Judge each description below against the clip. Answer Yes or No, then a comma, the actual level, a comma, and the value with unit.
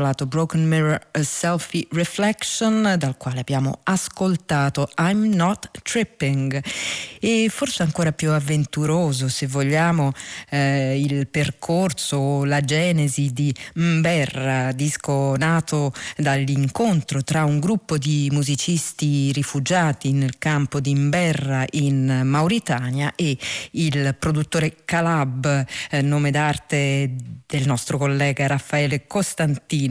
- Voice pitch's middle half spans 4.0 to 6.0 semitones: No, average, 3.0 semitones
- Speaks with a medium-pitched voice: Yes, medium, 145 Hz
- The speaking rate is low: Yes, slow, 110 wpm